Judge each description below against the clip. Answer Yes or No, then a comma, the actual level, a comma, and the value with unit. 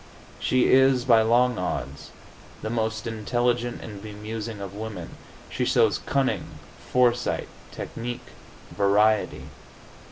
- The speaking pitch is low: Yes, low, 115 Hz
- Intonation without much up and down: Yes, narrow, 2.3 semitones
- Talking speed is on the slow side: Yes, slow, 105 wpm